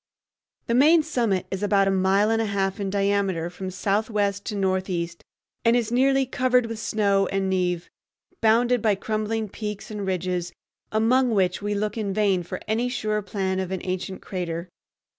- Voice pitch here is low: No, high, 200 Hz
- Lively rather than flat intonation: No, average, 2.9 semitones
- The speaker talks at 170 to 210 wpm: Yes, average, 175 wpm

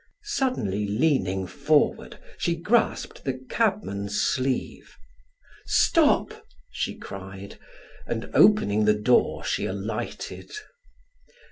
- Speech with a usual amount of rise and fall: No, wide, 8.7 semitones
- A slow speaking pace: Yes, slow, 90 wpm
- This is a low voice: Yes, low, 115 Hz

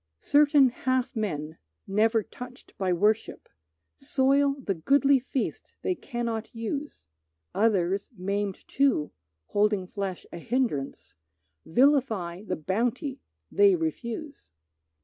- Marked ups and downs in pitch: Yes, wide, 5.9 semitones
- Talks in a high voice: Yes, high, 230 Hz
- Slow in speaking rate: Yes, slow, 105 wpm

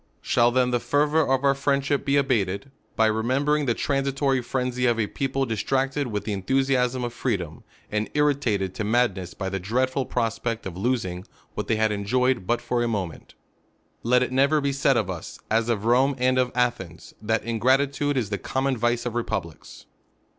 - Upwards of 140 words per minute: Yes, average, 185 wpm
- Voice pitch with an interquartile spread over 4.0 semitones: No, average, 3.7 semitones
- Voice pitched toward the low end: Yes, low, 125 Hz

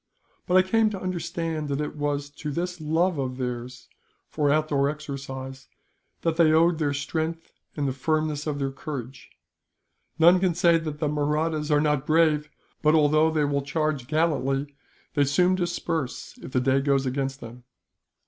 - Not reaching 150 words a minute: No, average, 165 wpm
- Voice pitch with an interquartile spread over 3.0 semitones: No, average, 2.7 semitones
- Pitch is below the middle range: No, medium, 150 Hz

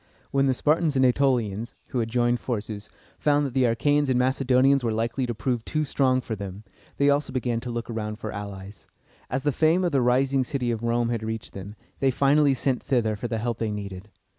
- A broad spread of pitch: No, average, 3.5 semitones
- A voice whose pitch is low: Yes, low, 120 Hz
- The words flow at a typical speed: No, fast, 215 wpm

